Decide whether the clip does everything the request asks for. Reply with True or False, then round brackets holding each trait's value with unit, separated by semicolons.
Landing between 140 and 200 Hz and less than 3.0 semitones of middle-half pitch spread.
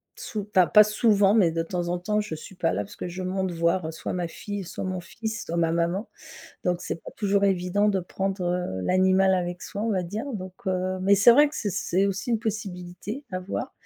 True (185 Hz; 2.5 semitones)